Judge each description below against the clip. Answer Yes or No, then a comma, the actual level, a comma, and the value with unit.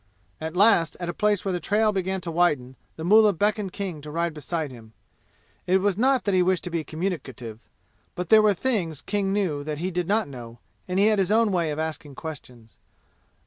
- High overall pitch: No, medium, 180 Hz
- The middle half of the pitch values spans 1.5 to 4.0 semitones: No, average, 4.5 semitones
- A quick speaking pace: Yes, fast, 215 wpm